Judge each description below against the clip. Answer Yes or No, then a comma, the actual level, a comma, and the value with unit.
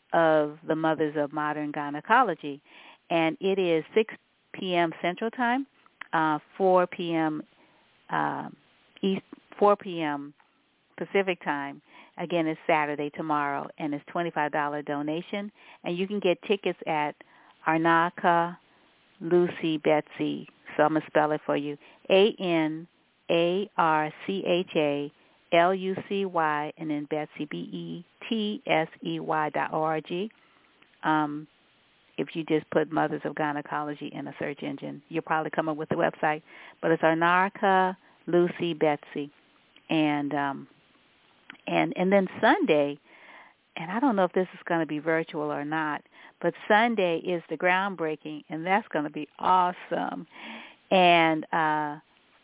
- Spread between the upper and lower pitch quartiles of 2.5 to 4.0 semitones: Yes, average, 3.4 semitones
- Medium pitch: Yes, medium, 160 Hz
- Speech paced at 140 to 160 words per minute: Yes, average, 145 wpm